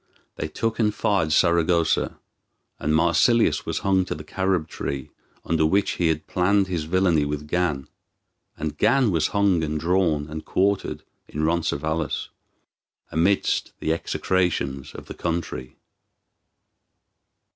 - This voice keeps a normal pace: No, slow, 130 wpm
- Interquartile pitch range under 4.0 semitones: Yes, average, 3.4 semitones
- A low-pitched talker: Yes, very low, 85 Hz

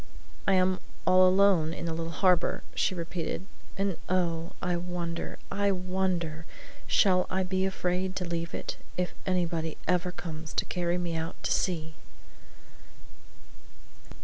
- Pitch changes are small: Yes, narrow, 1.8 semitones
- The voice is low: No, medium, 180 Hz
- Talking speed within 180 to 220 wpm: No, average, 140 wpm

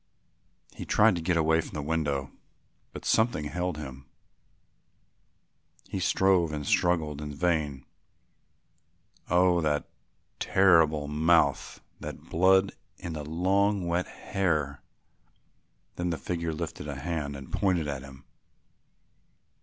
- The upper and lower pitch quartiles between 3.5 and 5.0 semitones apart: No, average, 3.1 semitones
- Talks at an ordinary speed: No, slow, 120 wpm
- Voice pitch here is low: Yes, very low, 80 Hz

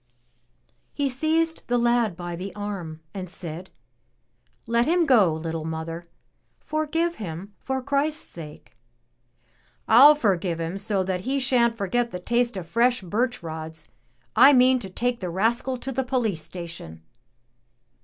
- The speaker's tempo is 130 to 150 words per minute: Yes, average, 145 wpm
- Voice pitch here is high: Yes, high, 220 Hz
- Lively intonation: Yes, wide, 6.7 semitones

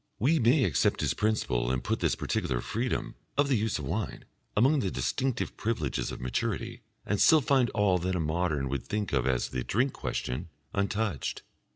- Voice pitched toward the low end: Yes, low, 100 Hz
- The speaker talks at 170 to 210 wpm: Yes, average, 185 wpm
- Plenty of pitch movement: Yes, wide, 8.3 semitones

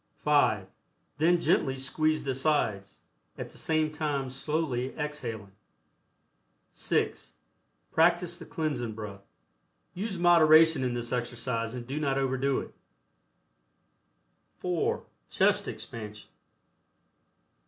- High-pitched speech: No, medium, 140 Hz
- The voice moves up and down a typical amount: Yes, average, 4.5 semitones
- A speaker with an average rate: No, slow, 100 wpm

